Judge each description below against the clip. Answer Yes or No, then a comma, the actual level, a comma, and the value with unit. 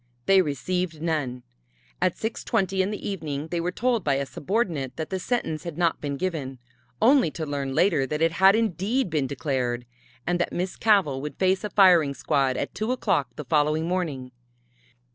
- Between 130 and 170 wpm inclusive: No, average, 180 wpm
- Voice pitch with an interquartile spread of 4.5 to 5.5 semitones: Yes, average, 5.1 semitones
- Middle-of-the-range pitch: Yes, medium, 165 Hz